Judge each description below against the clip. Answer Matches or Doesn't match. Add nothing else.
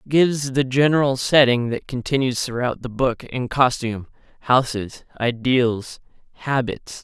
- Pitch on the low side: Matches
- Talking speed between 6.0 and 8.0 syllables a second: Doesn't match